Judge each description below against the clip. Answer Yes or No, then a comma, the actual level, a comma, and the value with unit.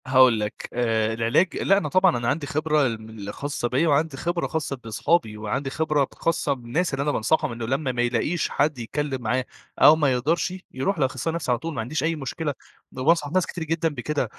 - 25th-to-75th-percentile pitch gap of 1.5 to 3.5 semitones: No, average, 4.7 semitones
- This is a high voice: No, medium, 140 Hz